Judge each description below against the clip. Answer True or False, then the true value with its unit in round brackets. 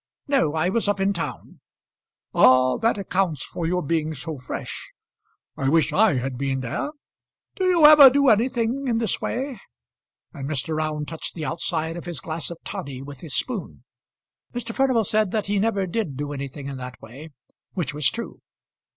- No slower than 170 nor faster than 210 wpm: True (180 wpm)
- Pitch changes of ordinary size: False (7.8 semitones)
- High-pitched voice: False (170 Hz)